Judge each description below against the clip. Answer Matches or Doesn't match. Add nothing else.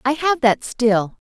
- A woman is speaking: Matches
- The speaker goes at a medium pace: Matches